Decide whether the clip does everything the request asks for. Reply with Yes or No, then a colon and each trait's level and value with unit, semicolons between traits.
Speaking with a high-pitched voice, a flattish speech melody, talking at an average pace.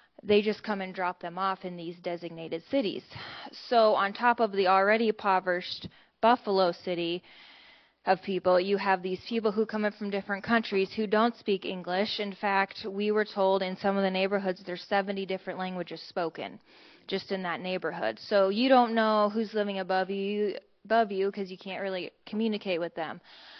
Yes: high, 195 Hz; narrow, 2.3 semitones; average, 185 wpm